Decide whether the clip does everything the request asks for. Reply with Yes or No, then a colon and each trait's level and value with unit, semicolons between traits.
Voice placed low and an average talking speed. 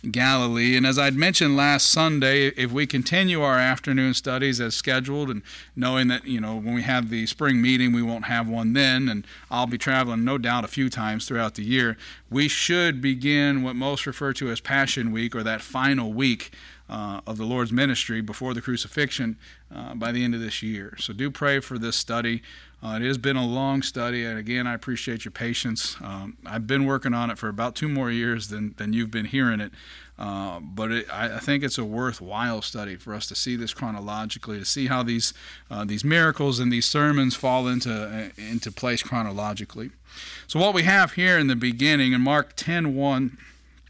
No: low, 125 Hz; fast, 210 wpm